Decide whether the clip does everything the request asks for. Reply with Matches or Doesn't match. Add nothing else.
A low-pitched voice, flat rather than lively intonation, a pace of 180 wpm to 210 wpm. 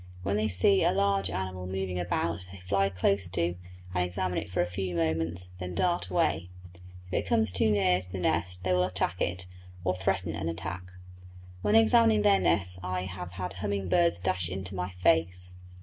Matches